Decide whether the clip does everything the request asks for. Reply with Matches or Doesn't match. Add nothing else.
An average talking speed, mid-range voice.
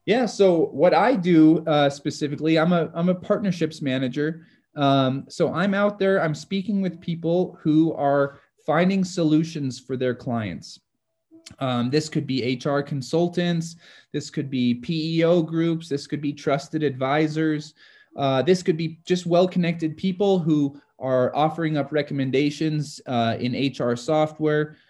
Matches